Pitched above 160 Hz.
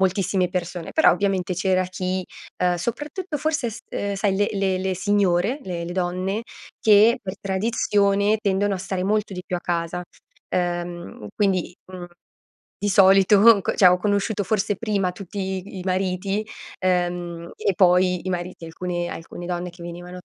Yes: medium, 185 Hz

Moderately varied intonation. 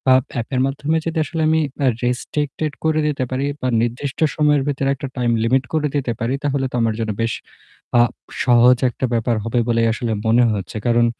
Yes: average, 3.4 semitones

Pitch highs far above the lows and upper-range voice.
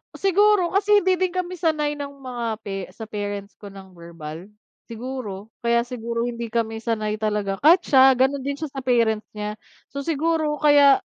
Yes: wide, 6.0 semitones; high, 245 Hz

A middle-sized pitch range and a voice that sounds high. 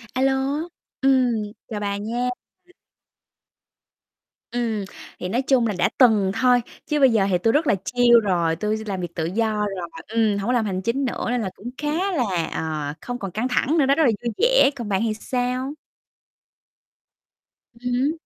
Yes: average, 4.3 semitones; high, 235 Hz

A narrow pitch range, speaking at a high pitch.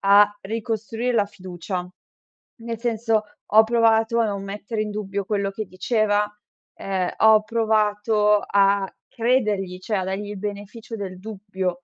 Yes: narrow, 2.1 semitones; high, 210 Hz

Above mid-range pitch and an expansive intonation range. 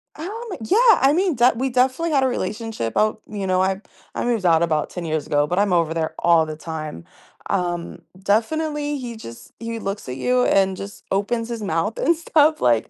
Yes: high, 205 Hz; wide, 6.9 semitones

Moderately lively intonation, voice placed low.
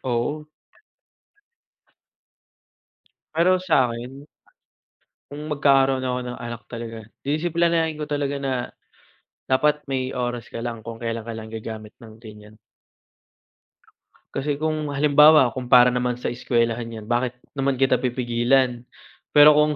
Yes: average, 3.7 semitones; low, 130 Hz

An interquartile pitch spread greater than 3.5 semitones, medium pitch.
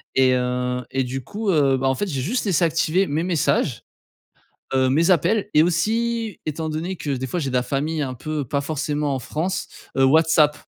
Yes: average, 4.3 semitones; medium, 150 Hz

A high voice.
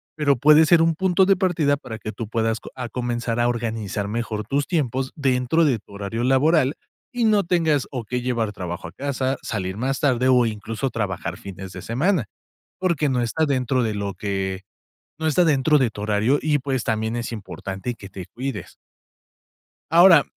No: low, 125 Hz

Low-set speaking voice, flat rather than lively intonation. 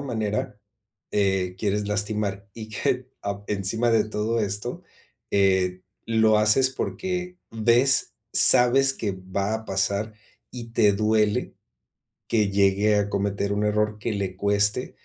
Yes: low, 105 Hz; narrow, 2.2 semitones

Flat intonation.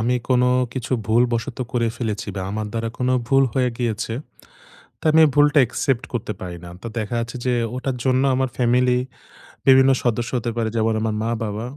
Yes: narrow, 2.3 semitones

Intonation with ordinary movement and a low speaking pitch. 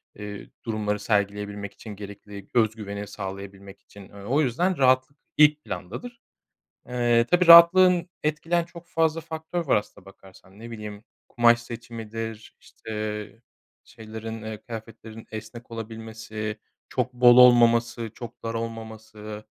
Yes: average, 3.3 semitones; low, 115 Hz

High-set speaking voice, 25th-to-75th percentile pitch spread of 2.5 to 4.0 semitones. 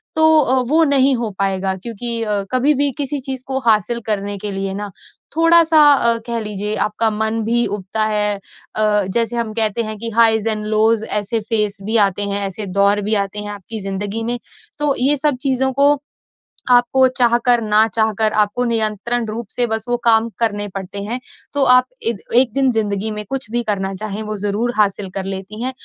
Yes: high, 220 Hz; average, 2.8 semitones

